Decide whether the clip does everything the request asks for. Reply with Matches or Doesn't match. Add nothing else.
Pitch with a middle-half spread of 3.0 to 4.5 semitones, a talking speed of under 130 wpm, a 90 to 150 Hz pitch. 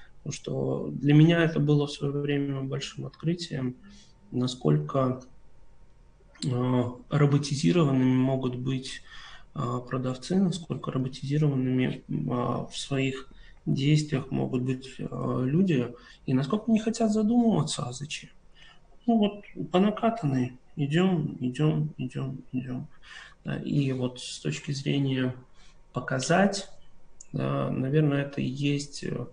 Matches